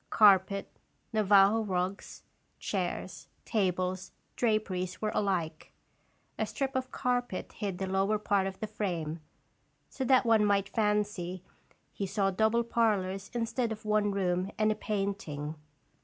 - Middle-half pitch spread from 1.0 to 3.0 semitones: Yes, narrow, 2.5 semitones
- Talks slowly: Yes, slow, 130 wpm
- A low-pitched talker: No, high, 200 Hz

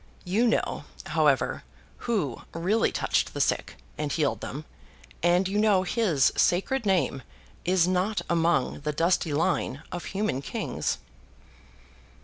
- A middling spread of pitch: Yes, average, 4.6 semitones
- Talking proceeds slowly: Yes, slow, 130 wpm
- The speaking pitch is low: No, medium, 175 Hz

